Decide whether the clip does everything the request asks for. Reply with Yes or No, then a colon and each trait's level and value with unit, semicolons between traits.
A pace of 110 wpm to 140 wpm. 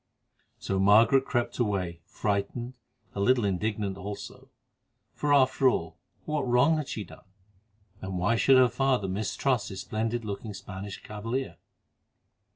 Yes: slow, 135 wpm